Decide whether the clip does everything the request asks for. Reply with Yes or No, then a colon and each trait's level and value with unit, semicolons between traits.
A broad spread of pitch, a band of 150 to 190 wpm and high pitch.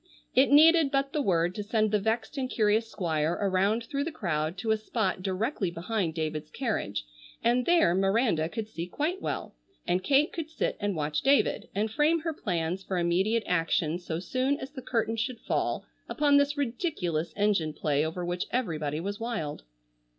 Yes: wide, 7.1 semitones; average, 180 wpm; high, 210 Hz